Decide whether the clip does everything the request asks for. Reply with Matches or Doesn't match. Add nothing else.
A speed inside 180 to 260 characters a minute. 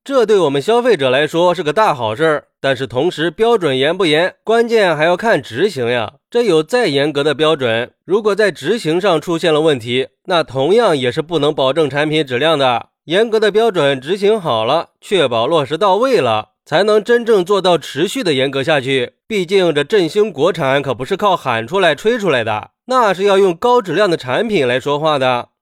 Doesn't match